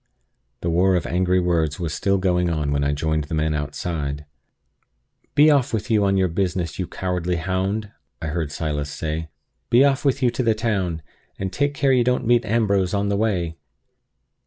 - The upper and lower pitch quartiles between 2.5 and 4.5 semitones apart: No, average, 5.3 semitones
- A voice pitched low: Yes, very low, 90 Hz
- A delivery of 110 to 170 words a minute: No, average, 190 wpm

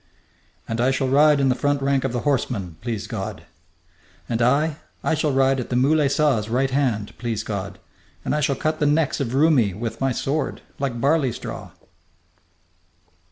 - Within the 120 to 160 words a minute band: No, average, 175 wpm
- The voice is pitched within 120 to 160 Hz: Yes, low, 135 Hz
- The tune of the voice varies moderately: Yes, average, 3.5 semitones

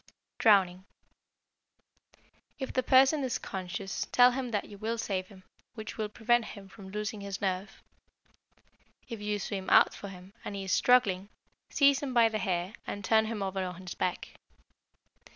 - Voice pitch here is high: Yes, high, 205 Hz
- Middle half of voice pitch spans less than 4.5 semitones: Yes, average, 3.3 semitones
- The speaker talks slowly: No, average, 170 wpm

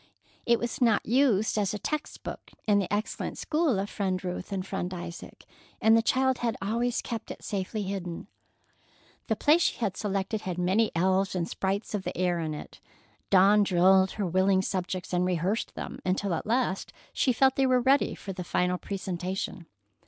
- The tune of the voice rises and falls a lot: No, average, 3.5 semitones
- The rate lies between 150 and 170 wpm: No, average, 185 wpm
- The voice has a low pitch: No, high, 195 Hz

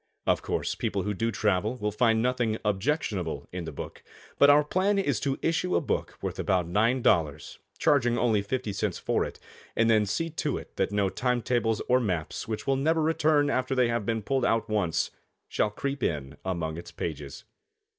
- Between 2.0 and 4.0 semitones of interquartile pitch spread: No, wide, 5.5 semitones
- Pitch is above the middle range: No, low, 115 Hz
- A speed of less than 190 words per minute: No, average, 195 wpm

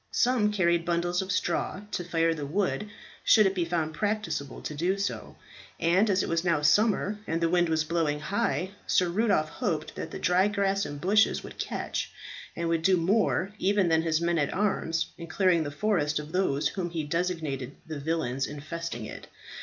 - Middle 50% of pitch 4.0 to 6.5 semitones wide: No, average, 3.5 semitones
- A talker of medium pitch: Yes, medium, 170 Hz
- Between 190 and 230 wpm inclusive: Yes, average, 195 wpm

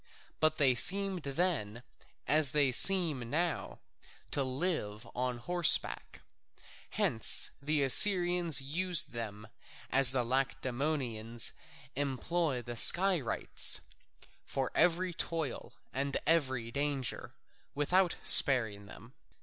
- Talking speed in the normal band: No, slow, 100 wpm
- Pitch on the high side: No, medium, 140 Hz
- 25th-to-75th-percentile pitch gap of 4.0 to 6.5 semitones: Yes, wide, 5.5 semitones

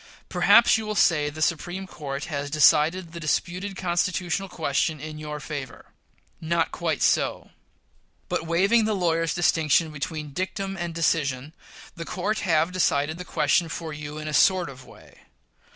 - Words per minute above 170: No, average, 155 wpm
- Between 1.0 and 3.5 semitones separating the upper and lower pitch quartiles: Yes, average, 3.0 semitones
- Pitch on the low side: No, medium, 165 Hz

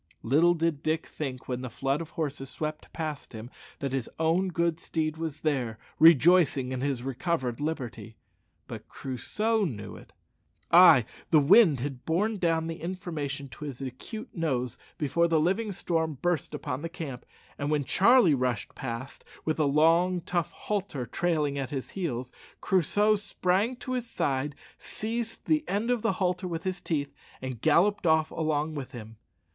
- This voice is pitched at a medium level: Yes, medium, 160 Hz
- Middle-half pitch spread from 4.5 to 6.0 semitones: Yes, average, 4.8 semitones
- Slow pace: No, average, 165 wpm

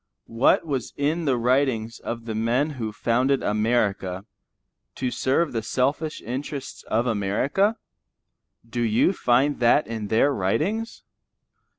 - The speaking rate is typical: No, slow, 125 wpm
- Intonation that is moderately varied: Yes, average, 4.2 semitones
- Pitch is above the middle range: No, low, 125 Hz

